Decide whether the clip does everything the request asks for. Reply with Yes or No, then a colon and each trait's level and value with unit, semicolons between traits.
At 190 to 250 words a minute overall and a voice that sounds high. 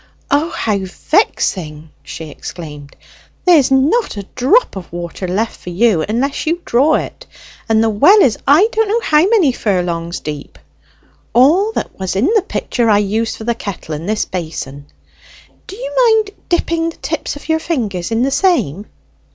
No: average, 170 wpm; high, 230 Hz